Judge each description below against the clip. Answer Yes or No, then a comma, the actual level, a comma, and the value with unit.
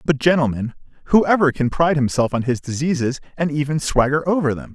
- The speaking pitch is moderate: Yes, medium, 145 Hz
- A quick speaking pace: No, average, 175 wpm